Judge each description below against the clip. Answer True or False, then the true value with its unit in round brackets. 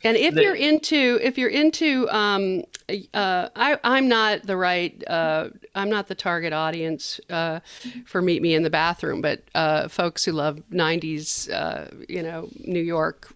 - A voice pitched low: False (180 Hz)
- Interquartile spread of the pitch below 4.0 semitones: False (5.6 semitones)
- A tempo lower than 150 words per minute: False (170 wpm)